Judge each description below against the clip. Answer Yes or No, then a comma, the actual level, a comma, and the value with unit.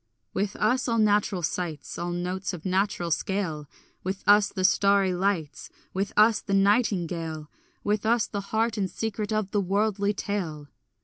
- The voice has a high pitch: Yes, high, 195 Hz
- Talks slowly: No, average, 160 wpm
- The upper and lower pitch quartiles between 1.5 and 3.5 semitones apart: Yes, average, 2.8 semitones